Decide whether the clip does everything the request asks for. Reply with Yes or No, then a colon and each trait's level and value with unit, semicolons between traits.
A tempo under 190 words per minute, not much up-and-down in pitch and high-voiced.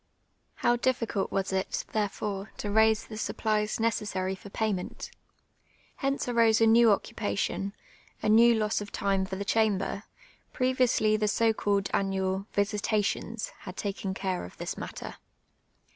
Yes: average, 150 wpm; narrow, 2.3 semitones; high, 210 Hz